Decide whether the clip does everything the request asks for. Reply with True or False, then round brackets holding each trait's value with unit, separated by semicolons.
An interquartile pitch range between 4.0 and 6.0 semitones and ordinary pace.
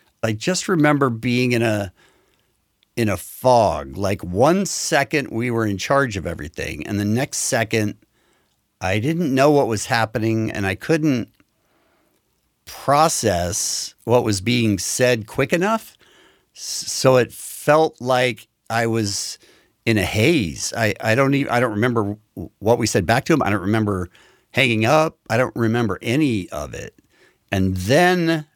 True (4.7 semitones; 155 wpm)